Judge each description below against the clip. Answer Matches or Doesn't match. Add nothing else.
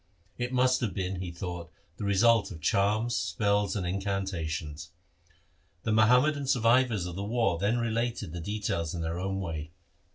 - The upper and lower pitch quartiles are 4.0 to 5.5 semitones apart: Matches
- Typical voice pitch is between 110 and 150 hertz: Doesn't match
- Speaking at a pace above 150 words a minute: Matches